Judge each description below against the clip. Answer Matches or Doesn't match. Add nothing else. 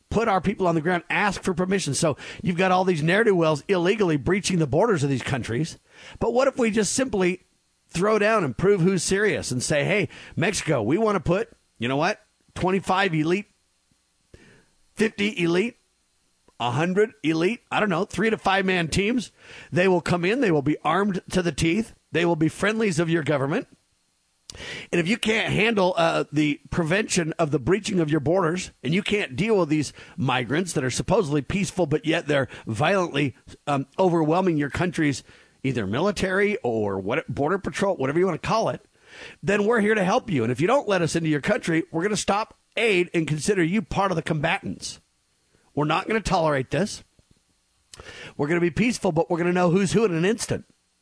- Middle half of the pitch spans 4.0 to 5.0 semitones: Matches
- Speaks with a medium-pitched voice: Matches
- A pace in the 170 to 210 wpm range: Matches